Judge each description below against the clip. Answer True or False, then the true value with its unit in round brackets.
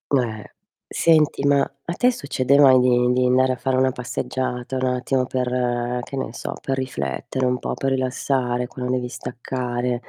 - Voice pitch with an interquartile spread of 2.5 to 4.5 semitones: False (1.2 semitones)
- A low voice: True (125 Hz)